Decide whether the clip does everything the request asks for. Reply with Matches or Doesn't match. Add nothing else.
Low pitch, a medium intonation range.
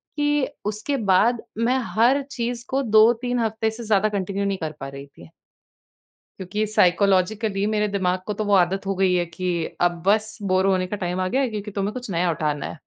Doesn't match